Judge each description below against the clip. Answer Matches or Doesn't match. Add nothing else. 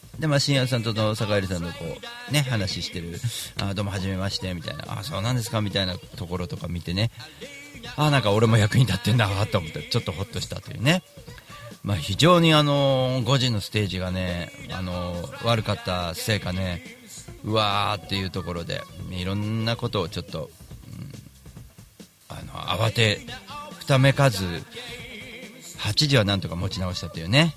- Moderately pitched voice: Doesn't match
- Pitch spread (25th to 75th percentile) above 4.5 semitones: Matches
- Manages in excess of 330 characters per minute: Doesn't match